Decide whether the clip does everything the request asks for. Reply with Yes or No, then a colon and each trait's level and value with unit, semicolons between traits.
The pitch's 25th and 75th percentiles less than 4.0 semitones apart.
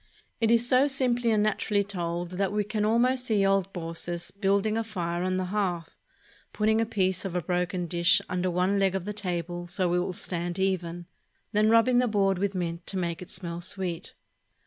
Yes: average, 3.2 semitones